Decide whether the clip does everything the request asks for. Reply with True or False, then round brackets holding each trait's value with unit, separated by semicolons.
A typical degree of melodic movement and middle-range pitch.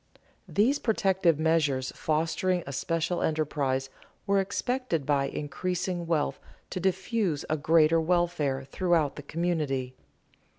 True (3.9 semitones; 165 Hz)